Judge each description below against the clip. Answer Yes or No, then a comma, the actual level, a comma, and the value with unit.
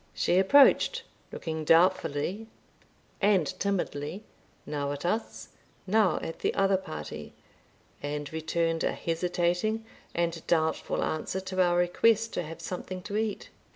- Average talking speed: No, slow, 125 wpm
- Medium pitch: Yes, medium, 175 Hz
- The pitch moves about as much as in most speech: Yes, average, 3.5 semitones